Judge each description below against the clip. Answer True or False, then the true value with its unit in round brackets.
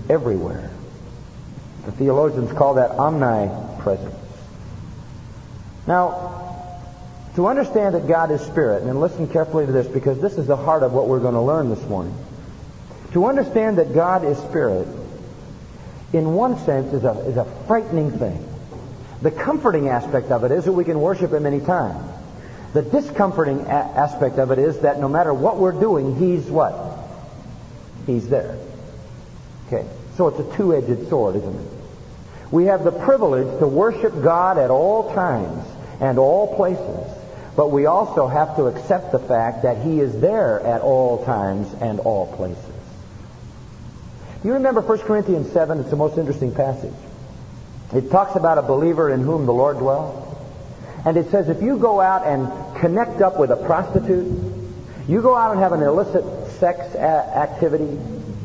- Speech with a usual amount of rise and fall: False (5.9 semitones)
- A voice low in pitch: False (150 Hz)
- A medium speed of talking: True (160 wpm)